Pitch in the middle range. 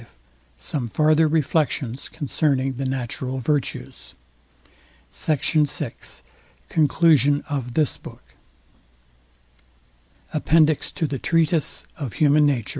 Yes: medium, 145 Hz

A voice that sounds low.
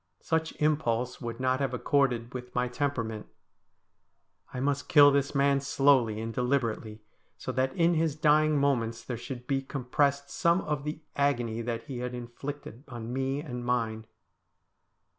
Yes: low, 130 Hz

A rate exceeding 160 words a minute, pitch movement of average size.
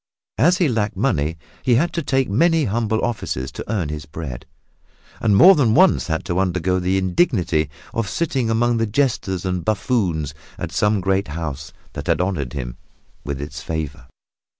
No: average, 175 wpm; wide, 6.9 semitones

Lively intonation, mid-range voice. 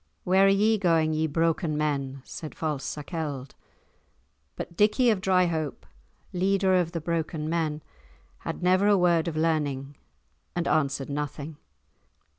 No: average, 3.4 semitones; medium, 165 Hz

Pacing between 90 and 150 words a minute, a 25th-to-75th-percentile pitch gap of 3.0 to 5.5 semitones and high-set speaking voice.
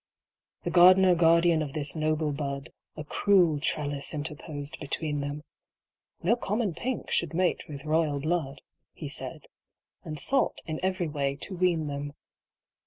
No: average, 145 wpm; average, 3.3 semitones; medium, 155 Hz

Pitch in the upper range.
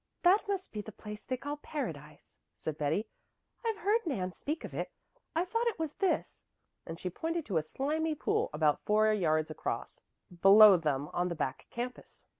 Yes: high, 215 Hz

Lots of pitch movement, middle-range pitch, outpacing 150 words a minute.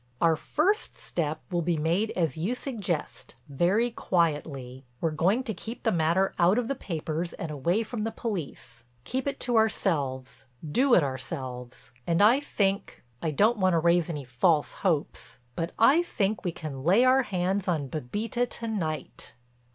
Yes: wide, 6.4 semitones; medium, 175 Hz; average, 160 wpm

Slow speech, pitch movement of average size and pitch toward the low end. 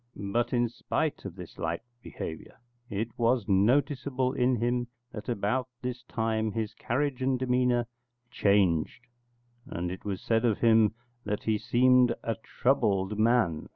No: average, 145 wpm; average, 3.4 semitones; low, 115 Hz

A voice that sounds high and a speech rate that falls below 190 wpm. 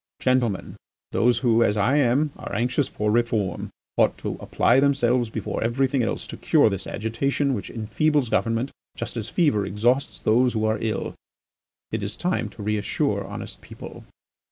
No: low, 115 Hz; average, 160 wpm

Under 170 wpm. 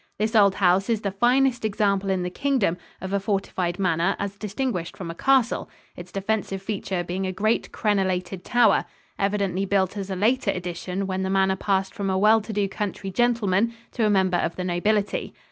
No: average, 195 wpm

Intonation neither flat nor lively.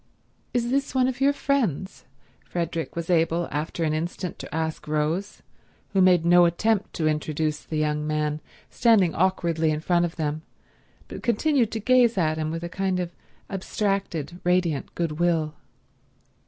Yes: average, 3.9 semitones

